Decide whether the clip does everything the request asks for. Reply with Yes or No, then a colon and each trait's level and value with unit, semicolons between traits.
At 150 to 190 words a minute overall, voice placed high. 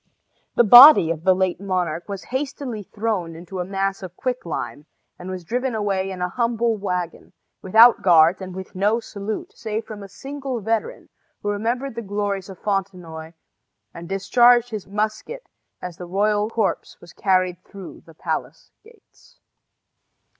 Yes: average, 160 wpm; high, 200 Hz